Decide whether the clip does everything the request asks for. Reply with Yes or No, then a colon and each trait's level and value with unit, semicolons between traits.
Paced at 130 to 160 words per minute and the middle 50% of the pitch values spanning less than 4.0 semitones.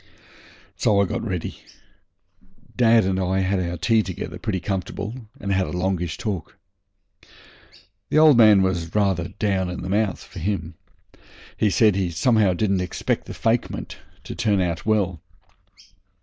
Yes: average, 150 wpm; average, 2.9 semitones